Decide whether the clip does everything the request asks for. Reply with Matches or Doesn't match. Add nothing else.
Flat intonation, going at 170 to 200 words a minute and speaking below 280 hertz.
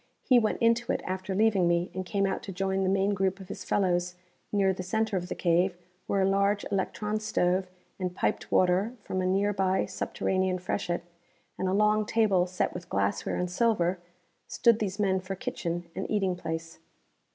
Matches